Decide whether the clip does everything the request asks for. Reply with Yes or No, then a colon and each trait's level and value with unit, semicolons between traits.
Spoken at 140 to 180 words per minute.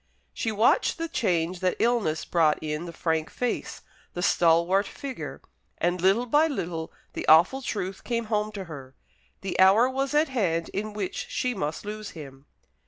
Yes: average, 170 wpm